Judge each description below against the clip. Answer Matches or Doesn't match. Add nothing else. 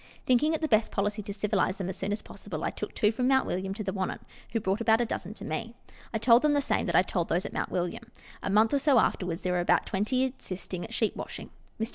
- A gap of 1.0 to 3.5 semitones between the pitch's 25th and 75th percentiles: Doesn't match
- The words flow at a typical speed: Doesn't match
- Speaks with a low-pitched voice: Doesn't match